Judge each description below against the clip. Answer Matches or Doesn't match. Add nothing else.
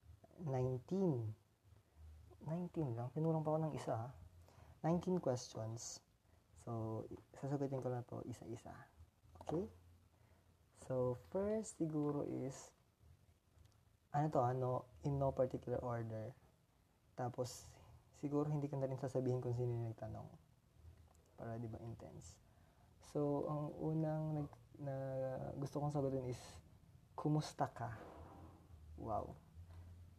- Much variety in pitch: Matches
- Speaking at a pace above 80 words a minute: Matches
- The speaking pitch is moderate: Doesn't match